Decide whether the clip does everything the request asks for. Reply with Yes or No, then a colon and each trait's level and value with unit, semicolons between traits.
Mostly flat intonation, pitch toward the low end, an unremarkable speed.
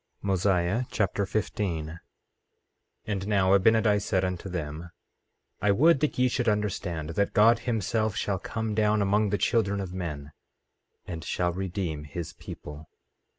No: average, 3.5 semitones; low, 100 Hz; average, 145 wpm